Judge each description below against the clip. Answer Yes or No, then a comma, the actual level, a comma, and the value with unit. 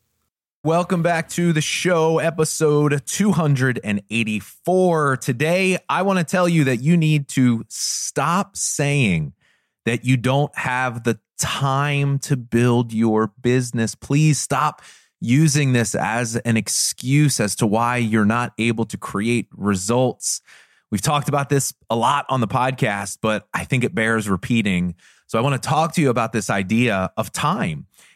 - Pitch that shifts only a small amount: No, average, 4.9 semitones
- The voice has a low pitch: Yes, low, 130 Hz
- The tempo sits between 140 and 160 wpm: Yes, average, 155 wpm